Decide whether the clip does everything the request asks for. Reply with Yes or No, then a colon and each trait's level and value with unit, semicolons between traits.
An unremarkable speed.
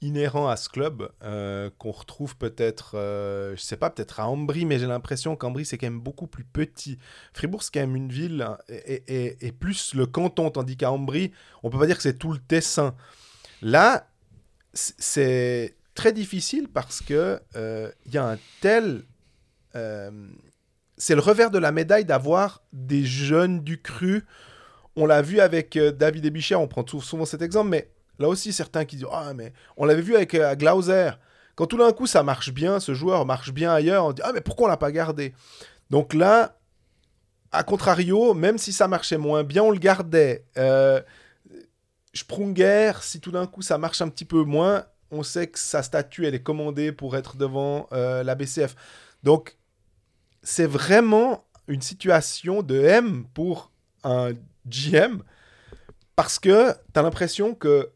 Yes: average, 185 wpm